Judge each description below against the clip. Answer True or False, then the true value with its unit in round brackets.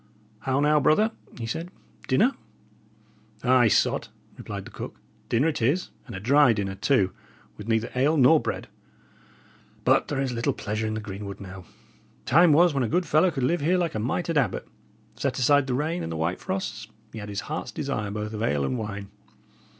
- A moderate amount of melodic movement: False (6.2 semitones)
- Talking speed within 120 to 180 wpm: False (195 wpm)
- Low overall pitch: True (125 Hz)